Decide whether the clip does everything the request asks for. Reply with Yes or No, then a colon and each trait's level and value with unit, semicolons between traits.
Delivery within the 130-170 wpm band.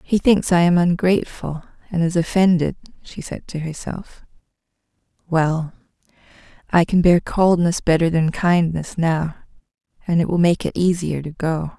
Yes: average, 150 wpm